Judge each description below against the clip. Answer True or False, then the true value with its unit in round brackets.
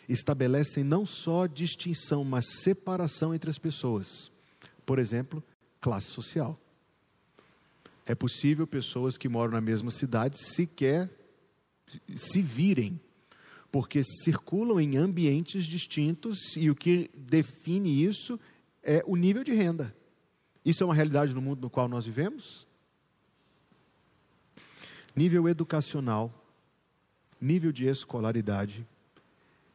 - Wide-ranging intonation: False (4.7 semitones)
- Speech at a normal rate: False (110 wpm)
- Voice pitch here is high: False (150 Hz)